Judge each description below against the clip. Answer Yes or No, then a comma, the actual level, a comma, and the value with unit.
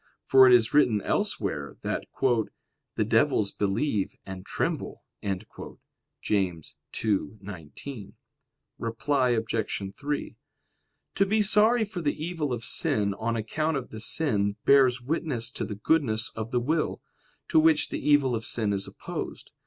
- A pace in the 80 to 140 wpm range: Yes, slow, 135 wpm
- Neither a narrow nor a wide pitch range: No, wide, 5.8 semitones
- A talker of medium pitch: No, low, 120 Hz